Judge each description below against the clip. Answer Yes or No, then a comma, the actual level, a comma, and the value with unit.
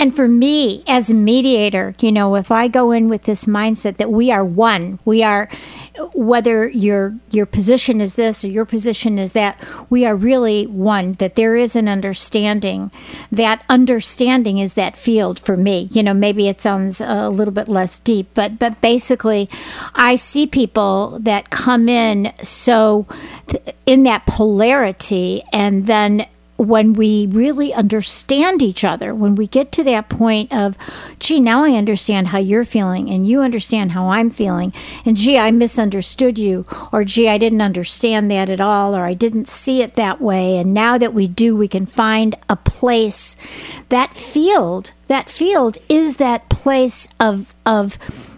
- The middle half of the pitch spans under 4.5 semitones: Yes, average, 2.9 semitones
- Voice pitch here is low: No, high, 220 Hz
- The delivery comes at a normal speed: Yes, average, 170 wpm